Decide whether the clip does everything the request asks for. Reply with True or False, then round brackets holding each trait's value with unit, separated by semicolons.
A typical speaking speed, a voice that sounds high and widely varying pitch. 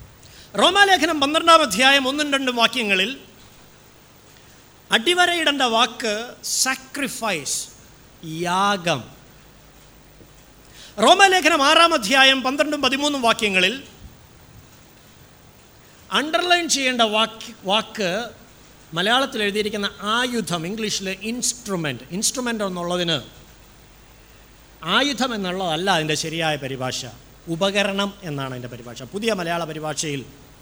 True (75 wpm; 210 Hz; 8.0 semitones)